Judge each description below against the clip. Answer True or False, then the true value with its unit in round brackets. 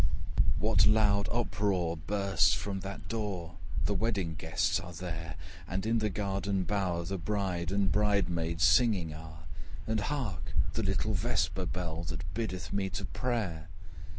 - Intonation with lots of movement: False (3.5 semitones)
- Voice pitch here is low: True (95 Hz)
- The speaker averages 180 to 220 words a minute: False (150 wpm)